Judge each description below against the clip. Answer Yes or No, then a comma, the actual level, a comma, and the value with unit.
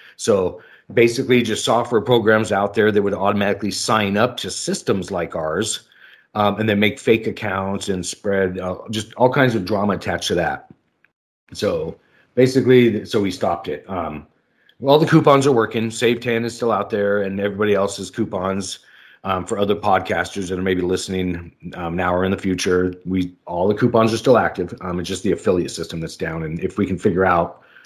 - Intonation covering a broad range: No, average, 3.3 semitones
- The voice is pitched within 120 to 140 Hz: No, low, 100 Hz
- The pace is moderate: Yes, average, 195 wpm